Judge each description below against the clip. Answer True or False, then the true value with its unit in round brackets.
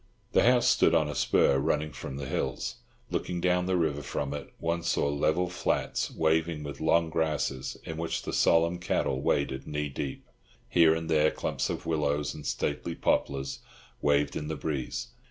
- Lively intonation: False (2.6 semitones)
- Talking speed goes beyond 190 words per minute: False (175 wpm)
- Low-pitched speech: True (75 Hz)